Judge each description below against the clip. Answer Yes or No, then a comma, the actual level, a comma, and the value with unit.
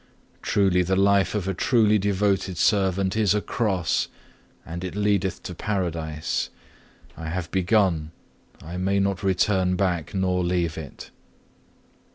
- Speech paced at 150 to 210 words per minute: No, slow, 135 wpm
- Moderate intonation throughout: No, narrow, 2.1 semitones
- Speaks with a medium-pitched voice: No, very low, 95 Hz